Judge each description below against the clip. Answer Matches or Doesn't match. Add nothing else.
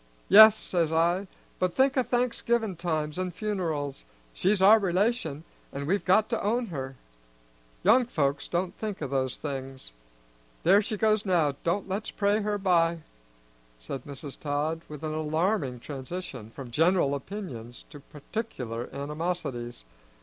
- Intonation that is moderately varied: Doesn't match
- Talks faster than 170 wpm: Doesn't match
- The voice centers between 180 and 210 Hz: Doesn't match